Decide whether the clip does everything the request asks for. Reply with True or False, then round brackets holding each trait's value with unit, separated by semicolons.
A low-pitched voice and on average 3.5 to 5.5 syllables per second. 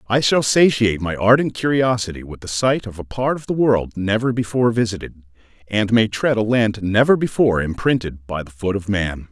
True (110 Hz; 5.4 syllables/s)